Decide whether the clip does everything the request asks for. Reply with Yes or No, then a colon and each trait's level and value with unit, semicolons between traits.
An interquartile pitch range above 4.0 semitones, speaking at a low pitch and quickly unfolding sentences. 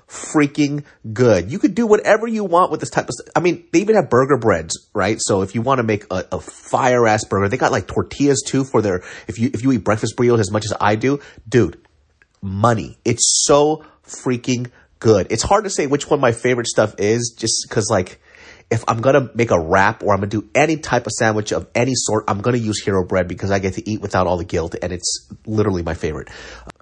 Yes: average, 5.1 semitones; low, 115 Hz; fast, 240 wpm